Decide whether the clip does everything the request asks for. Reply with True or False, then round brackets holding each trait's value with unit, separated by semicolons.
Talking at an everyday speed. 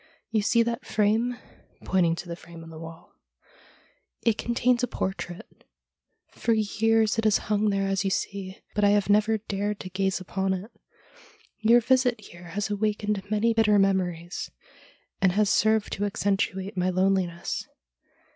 True (170 wpm)